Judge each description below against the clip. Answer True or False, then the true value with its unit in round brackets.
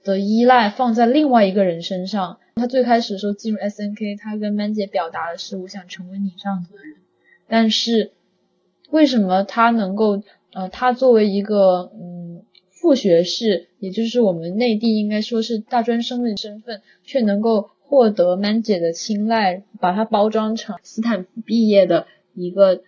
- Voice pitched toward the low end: False (210 Hz)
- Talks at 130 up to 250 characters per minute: False (275 characters per minute)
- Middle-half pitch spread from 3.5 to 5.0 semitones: False (3.0 semitones)